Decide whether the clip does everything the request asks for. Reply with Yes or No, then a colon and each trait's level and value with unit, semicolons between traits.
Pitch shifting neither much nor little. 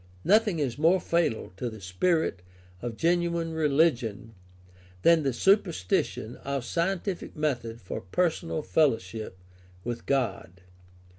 No: wide, 6.8 semitones